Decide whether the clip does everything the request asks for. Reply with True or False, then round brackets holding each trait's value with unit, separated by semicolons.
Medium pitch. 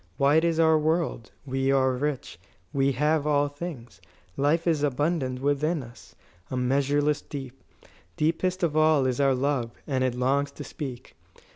True (145 Hz)